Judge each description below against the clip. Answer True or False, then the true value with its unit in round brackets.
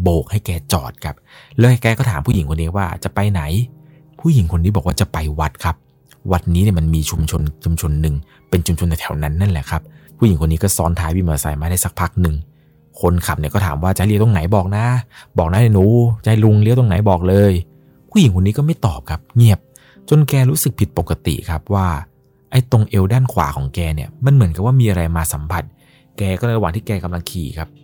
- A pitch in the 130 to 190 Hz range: False (95 Hz)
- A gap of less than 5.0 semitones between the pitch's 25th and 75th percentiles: False (5.6 semitones)